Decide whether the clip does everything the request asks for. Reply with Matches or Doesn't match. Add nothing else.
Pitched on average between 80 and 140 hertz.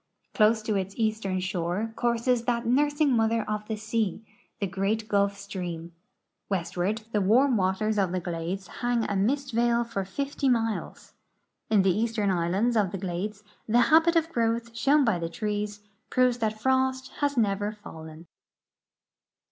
Doesn't match